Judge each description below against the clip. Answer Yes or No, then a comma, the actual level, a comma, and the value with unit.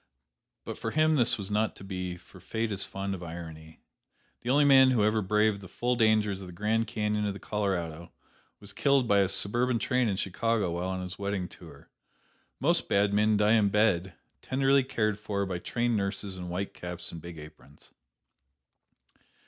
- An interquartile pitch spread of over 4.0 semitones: No, average, 3.3 semitones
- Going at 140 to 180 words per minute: No, average, 190 wpm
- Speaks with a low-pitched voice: Yes, low, 100 Hz